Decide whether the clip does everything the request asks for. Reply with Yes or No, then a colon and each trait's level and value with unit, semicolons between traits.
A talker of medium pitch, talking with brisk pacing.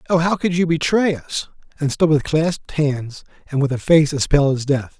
Yes: medium, 150 Hz; fast, 215 wpm